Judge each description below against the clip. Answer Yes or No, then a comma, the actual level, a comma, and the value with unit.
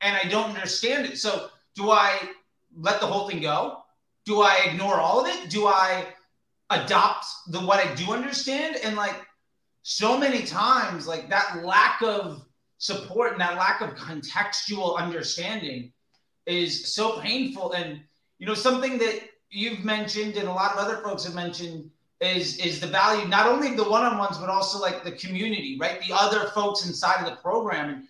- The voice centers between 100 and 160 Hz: No, high, 200 Hz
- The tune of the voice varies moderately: Yes, average, 3.6 semitones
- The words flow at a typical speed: Yes, average, 180 wpm